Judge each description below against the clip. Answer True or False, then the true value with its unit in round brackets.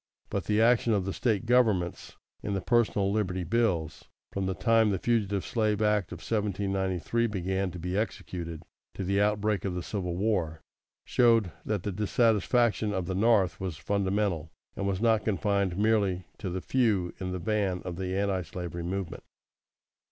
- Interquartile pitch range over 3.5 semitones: False (2.8 semitones)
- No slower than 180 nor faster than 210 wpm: False (165 wpm)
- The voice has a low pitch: True (100 Hz)